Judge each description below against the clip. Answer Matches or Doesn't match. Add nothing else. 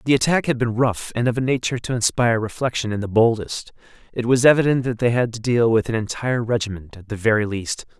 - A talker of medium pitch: Doesn't match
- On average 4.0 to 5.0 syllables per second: Doesn't match